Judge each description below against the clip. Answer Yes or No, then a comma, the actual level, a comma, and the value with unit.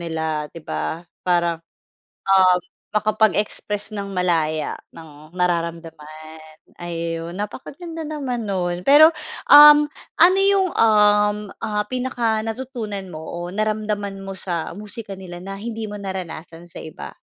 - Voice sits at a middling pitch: No, high, 195 Hz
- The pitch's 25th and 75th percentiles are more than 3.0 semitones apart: Yes, average, 4.5 semitones